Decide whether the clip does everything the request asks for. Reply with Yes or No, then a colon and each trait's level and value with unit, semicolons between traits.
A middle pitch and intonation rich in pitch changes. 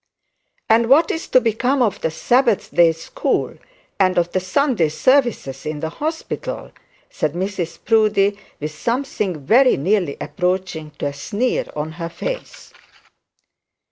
No: high, 195 Hz; wide, 7.2 semitones